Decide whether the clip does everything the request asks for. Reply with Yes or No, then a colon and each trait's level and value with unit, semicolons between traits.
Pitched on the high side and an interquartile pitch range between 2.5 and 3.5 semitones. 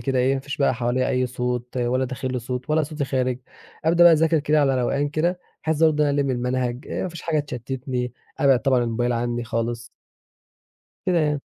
No: low, 130 Hz; average, 3.2 semitones